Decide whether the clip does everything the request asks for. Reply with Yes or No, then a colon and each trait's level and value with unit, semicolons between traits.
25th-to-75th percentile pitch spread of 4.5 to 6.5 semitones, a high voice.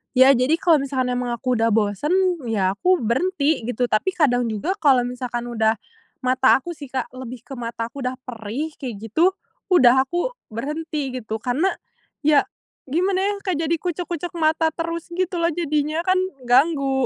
Yes: average, 5.3 semitones; very high, 270 Hz